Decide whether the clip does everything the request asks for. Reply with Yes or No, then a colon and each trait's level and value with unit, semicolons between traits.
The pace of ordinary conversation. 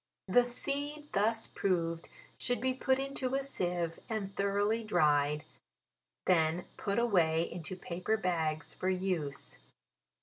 No: slow, 125 wpm